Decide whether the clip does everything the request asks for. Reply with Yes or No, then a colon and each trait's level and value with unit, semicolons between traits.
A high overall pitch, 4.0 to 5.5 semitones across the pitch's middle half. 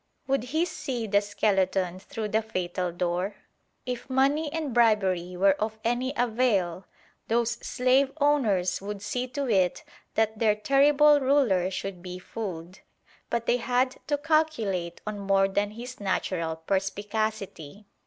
Yes: high, 215 Hz; average, 5.1 semitones